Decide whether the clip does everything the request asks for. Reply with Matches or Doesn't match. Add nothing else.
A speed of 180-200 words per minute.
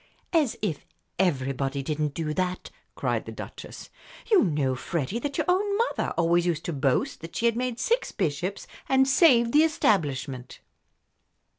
Doesn't match